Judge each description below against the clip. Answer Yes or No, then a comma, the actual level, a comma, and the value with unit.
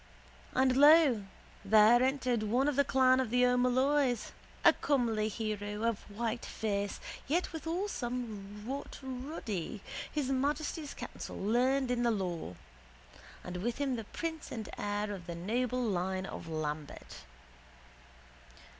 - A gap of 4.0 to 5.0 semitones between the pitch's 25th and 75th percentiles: Yes, average, 4.3 semitones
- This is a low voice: No, high, 240 Hz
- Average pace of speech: No, slow, 130 wpm